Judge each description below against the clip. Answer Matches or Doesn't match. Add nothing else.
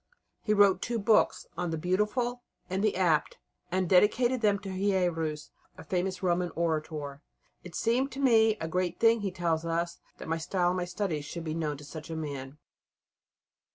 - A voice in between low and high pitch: Matches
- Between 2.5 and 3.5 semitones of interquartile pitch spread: Doesn't match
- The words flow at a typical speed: Matches